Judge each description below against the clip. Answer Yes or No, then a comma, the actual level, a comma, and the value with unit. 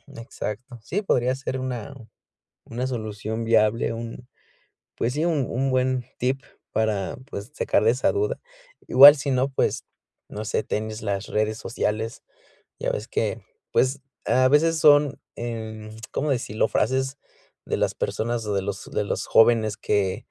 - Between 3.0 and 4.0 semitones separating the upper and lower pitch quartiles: Yes, average, 3.5 semitones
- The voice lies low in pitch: Yes, low, 120 Hz